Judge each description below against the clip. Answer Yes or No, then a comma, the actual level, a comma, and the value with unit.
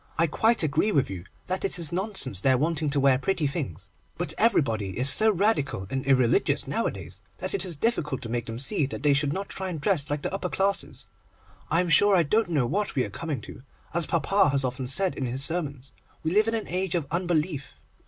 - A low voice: No, medium, 150 Hz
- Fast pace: Yes, fast, 225 wpm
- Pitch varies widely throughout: Yes, wide, 5.9 semitones